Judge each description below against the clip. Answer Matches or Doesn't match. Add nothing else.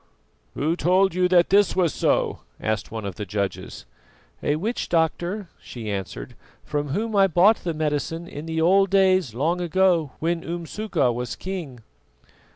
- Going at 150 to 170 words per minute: Matches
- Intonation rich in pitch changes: Doesn't match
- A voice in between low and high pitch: Matches